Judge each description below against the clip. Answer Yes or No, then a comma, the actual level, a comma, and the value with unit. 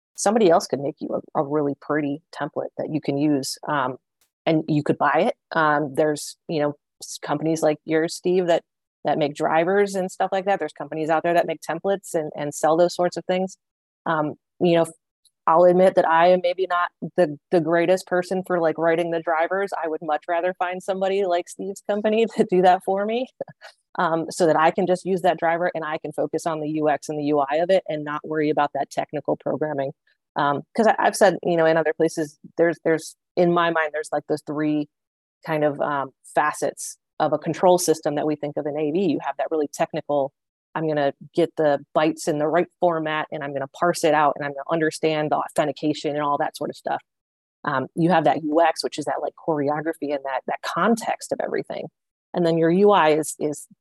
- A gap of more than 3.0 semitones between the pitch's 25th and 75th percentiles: No, average, 2.7 semitones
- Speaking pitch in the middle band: Yes, medium, 160 Hz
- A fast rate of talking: Yes, fast, 225 wpm